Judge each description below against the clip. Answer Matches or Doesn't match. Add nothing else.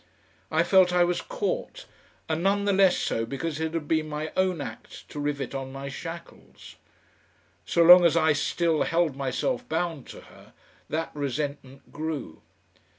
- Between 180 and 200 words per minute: Doesn't match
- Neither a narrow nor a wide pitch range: Matches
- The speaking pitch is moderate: Matches